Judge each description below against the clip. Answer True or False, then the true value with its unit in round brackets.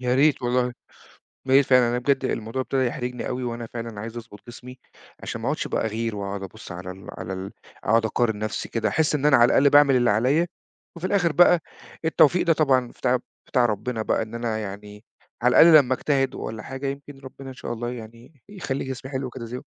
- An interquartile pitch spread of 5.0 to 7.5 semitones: False (3.3 semitones)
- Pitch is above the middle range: False (125 Hz)